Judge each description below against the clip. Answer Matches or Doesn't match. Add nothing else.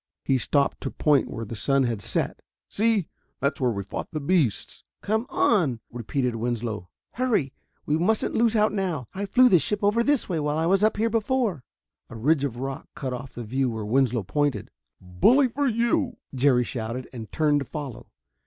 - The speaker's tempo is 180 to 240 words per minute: Matches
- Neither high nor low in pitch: Matches